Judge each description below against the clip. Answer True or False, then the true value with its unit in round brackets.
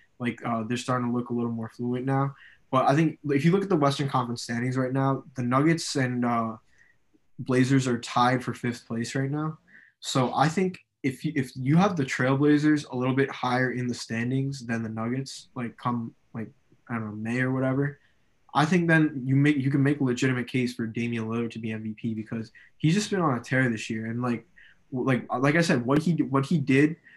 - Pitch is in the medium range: False (130 Hz)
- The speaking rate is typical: False (225 wpm)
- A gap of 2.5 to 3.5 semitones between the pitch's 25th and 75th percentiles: True (3.0 semitones)